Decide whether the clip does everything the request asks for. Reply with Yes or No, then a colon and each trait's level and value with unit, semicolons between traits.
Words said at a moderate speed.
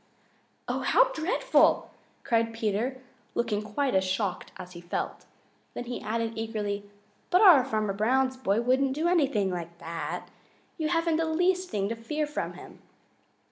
Yes: average, 155 wpm